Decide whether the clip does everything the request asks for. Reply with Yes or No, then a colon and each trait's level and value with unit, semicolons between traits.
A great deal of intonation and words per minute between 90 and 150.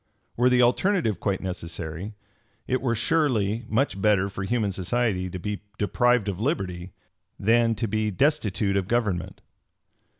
No: average, 4.0 semitones; average, 140 wpm